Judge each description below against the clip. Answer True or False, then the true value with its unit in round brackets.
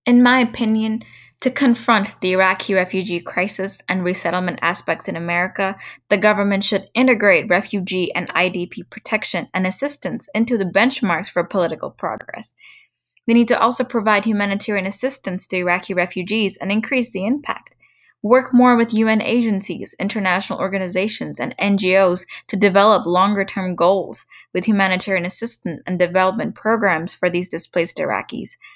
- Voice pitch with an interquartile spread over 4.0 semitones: False (3.3 semitones)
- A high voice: True (195 Hz)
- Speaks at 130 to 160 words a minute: True (140 wpm)